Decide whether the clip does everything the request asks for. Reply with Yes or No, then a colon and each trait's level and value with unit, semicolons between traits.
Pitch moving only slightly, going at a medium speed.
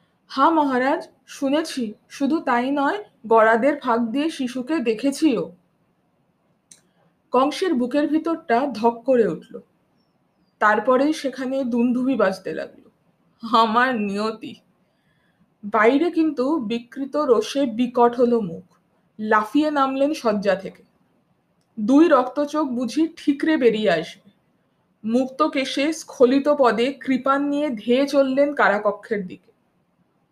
No: average, 4.3 semitones; average, 100 wpm